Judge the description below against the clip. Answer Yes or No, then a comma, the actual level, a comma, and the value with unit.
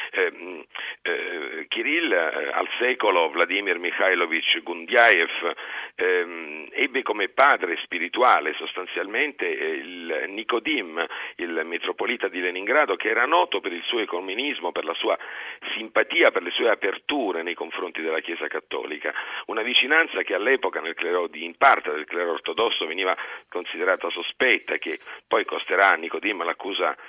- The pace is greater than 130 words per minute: Yes, average, 140 wpm